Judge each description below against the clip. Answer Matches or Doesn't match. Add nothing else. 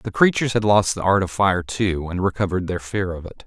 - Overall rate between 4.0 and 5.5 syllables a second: Doesn't match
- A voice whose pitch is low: Matches